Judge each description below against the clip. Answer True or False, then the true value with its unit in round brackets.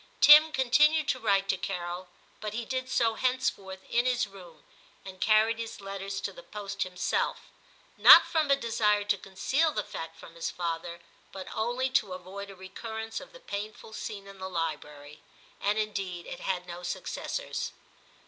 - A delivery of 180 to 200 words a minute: False (170 wpm)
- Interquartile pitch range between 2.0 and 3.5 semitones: False (4.1 semitones)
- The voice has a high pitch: True (200 Hz)